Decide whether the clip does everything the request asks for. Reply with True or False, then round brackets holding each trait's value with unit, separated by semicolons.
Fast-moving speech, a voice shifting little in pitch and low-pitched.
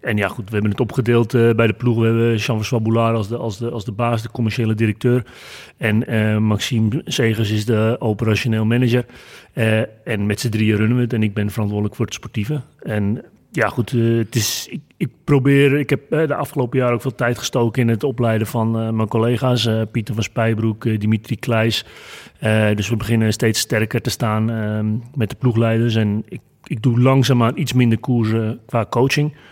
True (210 wpm; 2.0 semitones; 115 Hz)